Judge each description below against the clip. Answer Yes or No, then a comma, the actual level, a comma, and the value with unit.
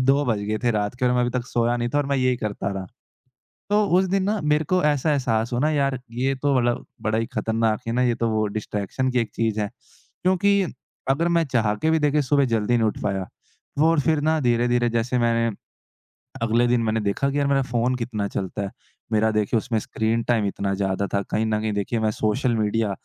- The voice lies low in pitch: Yes, low, 120 Hz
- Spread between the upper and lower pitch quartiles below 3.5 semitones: No, average, 4.0 semitones